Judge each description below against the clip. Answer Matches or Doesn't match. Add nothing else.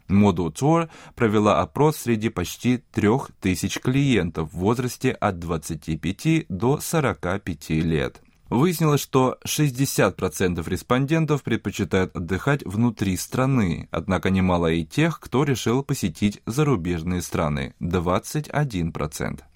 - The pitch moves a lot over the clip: Matches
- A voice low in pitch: Matches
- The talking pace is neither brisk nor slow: Doesn't match